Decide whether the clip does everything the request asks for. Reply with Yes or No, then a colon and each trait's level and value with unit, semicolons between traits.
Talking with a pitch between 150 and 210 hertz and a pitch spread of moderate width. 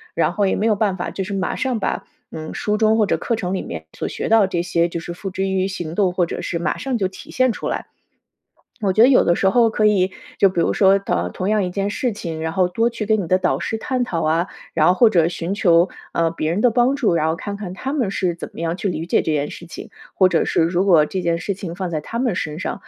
Yes: high, 190 Hz; average, 3.9 semitones